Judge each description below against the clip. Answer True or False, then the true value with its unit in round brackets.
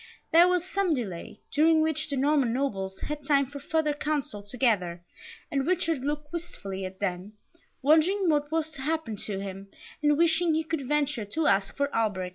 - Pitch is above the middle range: True (285 Hz)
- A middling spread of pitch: False (7.3 semitones)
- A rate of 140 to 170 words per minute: False (180 wpm)